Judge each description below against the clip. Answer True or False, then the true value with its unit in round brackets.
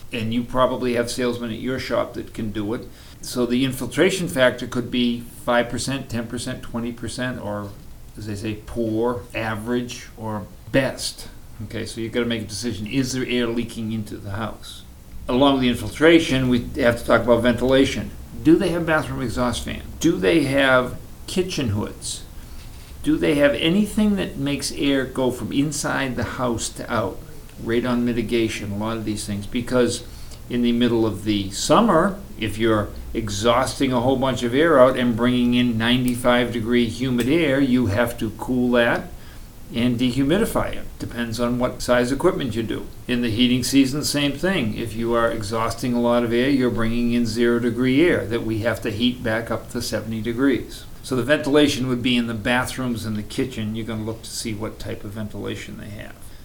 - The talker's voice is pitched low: True (120 Hz)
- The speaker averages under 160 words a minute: False (190 wpm)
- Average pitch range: False (2.2 semitones)